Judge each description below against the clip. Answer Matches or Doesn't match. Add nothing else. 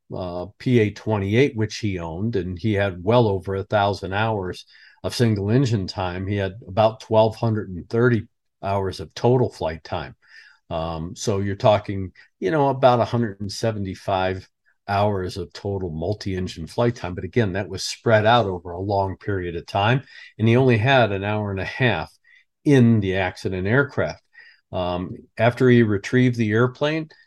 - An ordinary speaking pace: Matches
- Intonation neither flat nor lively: Matches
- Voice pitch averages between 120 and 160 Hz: Doesn't match